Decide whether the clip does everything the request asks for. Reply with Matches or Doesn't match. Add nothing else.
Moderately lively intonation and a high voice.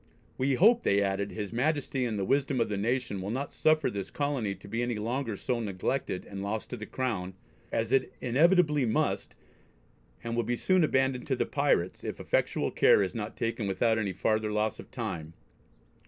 Doesn't match